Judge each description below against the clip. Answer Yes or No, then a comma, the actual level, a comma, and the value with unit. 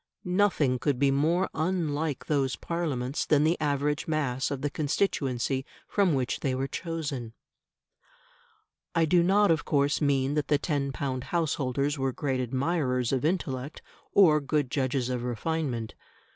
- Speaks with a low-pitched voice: No, medium, 145 Hz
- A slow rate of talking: No, average, 145 wpm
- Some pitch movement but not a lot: Yes, average, 3.5 semitones